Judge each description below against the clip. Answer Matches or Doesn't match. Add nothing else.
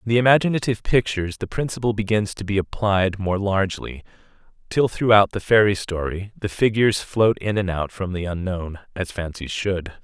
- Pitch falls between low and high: Doesn't match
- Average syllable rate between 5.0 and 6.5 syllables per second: Matches